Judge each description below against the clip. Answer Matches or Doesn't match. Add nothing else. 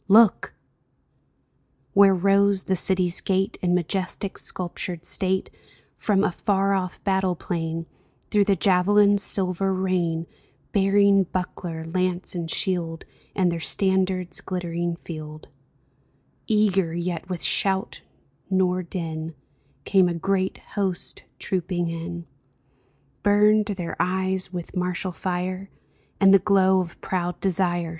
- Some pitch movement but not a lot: Doesn't match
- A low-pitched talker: Doesn't match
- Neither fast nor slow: Doesn't match